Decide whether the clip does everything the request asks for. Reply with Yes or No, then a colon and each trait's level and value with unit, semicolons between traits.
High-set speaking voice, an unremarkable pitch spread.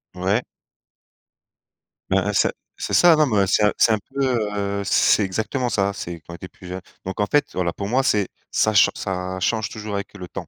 No: low, 100 Hz; average, 3.0 semitones